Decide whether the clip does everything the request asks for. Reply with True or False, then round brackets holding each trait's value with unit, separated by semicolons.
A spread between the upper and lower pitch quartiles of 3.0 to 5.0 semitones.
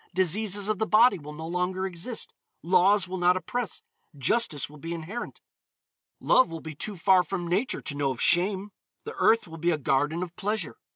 True (4.0 semitones)